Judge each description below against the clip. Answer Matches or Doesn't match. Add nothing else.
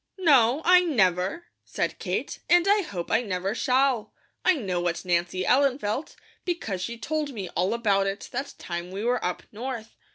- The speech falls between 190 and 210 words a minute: Doesn't match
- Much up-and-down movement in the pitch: Matches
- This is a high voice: Matches